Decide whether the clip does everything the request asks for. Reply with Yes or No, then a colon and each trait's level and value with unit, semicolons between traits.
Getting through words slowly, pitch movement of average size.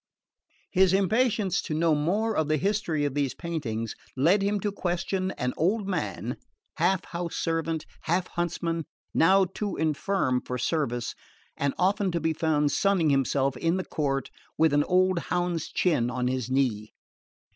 No: average, 155 wpm; average, 4.8 semitones